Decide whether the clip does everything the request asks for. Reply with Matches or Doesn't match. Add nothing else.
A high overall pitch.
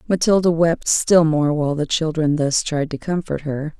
Doesn't match